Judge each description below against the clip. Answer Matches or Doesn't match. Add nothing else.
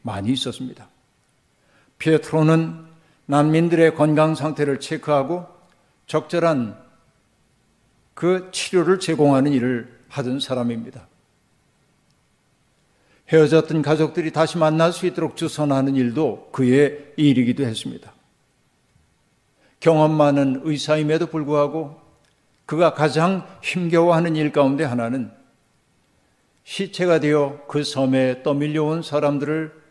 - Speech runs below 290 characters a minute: Matches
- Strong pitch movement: Doesn't match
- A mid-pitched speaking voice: Matches